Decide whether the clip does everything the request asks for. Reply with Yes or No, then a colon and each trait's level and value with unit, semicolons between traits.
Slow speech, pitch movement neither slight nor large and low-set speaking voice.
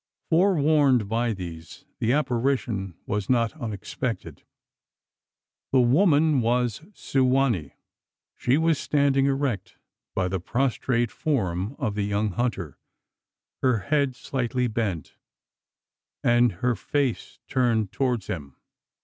Yes: slow, 115 wpm; average, 4.6 semitones; low, 120 Hz